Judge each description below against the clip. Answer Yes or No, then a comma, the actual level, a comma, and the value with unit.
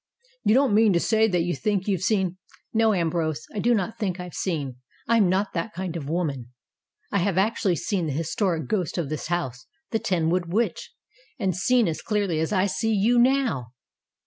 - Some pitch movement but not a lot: Yes, average, 4.5 semitones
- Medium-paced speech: No, fast, 210 wpm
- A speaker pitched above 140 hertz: Yes, medium, 185 Hz